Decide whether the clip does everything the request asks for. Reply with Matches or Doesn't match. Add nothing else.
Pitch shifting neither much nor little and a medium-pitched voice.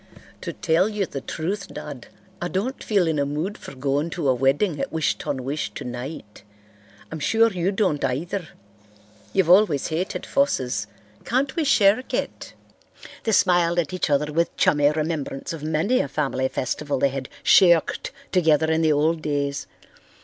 Matches